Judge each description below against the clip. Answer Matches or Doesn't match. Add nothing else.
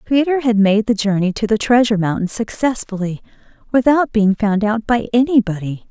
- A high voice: Matches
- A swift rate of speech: Doesn't match